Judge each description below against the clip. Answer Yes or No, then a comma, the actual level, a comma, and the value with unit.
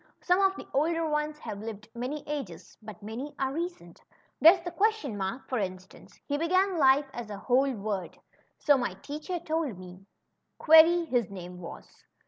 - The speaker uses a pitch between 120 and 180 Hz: No, very high, 270 Hz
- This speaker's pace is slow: No, average, 175 wpm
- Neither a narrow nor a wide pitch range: No, wide, 7.7 semitones